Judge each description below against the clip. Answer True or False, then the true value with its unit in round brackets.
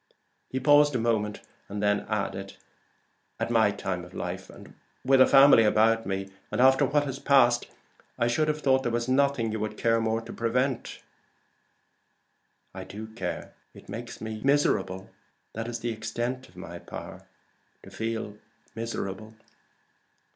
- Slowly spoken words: False (155 wpm)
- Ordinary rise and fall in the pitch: True (3.4 semitones)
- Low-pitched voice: True (115 Hz)